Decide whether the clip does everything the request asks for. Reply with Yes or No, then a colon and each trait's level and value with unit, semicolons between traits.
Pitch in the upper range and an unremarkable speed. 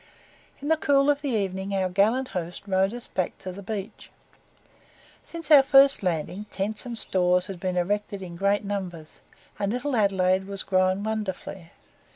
Yes: high, 200 Hz; average, 170 wpm